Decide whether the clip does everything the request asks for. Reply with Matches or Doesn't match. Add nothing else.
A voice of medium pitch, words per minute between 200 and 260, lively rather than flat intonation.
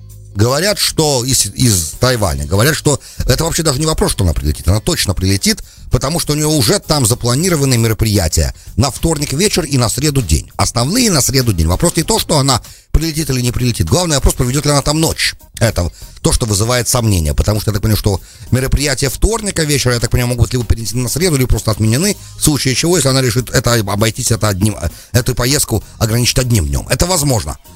Doesn't match